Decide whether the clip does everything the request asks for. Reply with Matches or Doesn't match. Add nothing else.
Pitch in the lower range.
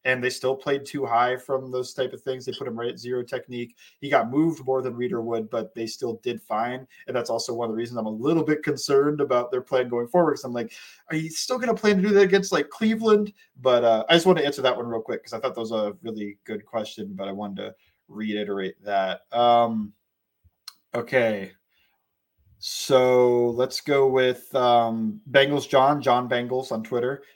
Matches